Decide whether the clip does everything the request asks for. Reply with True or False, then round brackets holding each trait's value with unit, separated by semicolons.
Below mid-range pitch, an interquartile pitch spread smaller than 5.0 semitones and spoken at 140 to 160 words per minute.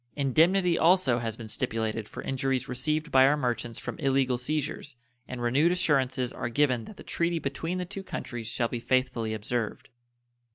False (130 Hz; 4.4 semitones; 170 wpm)